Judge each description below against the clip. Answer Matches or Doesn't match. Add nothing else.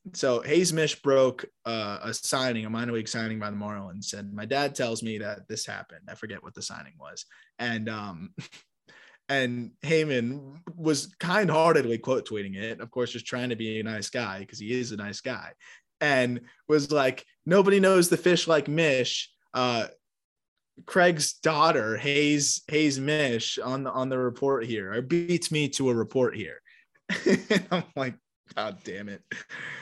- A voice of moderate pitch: Doesn't match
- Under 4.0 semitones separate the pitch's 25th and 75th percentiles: Doesn't match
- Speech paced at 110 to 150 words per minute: Doesn't match